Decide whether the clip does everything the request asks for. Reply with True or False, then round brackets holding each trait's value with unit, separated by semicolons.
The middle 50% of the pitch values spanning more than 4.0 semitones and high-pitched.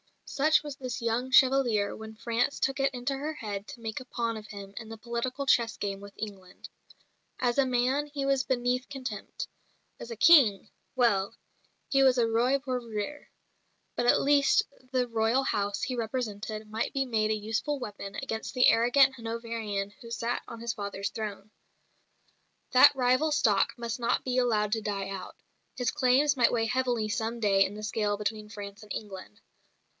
False (3.4 semitones; 230 Hz)